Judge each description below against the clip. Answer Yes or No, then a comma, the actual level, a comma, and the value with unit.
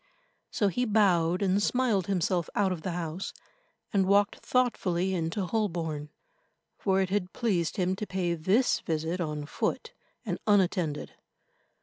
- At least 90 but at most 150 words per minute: Yes, average, 140 wpm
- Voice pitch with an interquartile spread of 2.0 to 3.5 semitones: Yes, average, 3.2 semitones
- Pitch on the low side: No, medium, 185 Hz